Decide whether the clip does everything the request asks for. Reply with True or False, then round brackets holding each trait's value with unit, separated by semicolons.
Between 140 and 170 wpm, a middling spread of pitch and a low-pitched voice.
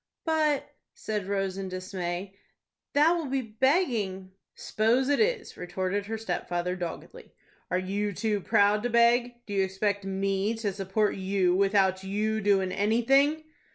False (150 wpm; 3.7 semitones; 205 Hz)